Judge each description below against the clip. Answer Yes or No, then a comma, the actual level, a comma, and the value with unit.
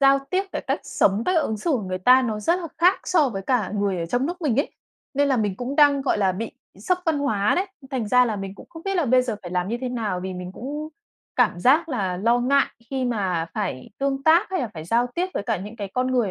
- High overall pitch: Yes, high, 245 Hz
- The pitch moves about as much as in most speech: No, wide, 5.9 semitones